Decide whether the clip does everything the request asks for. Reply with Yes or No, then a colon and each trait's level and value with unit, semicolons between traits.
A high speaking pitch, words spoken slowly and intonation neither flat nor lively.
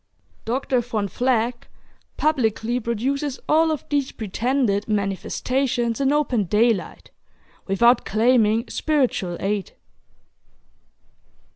Yes: high, 235 Hz; slow, 90 wpm; average, 3.9 semitones